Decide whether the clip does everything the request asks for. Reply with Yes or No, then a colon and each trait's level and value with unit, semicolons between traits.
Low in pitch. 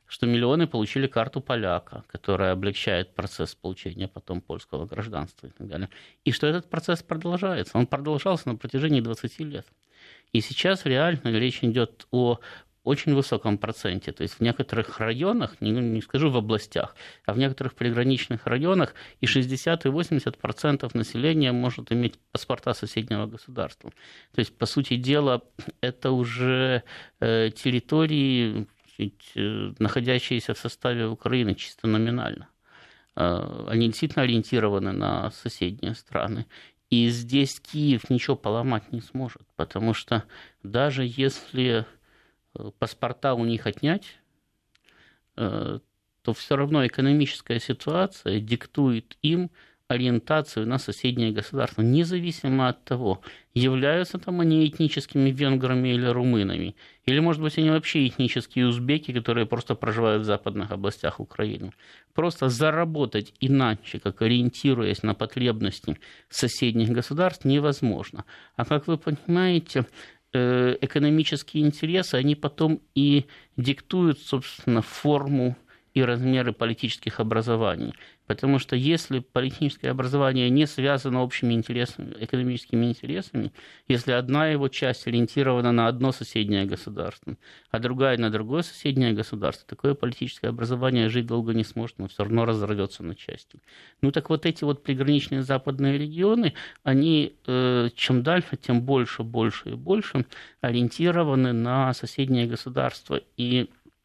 Yes: low, 125 Hz